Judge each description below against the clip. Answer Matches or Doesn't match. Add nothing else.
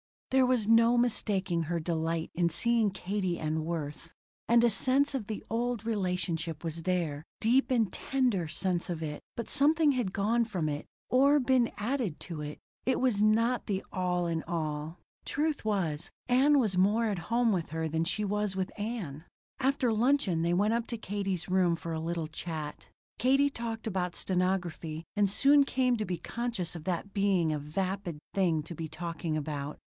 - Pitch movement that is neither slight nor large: Doesn't match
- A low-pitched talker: Doesn't match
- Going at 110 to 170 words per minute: Doesn't match